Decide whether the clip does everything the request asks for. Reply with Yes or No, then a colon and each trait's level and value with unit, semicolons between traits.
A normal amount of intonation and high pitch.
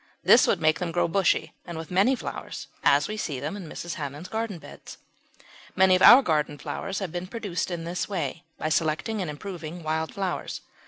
No: average, 3.7 semitones; medium, 175 Hz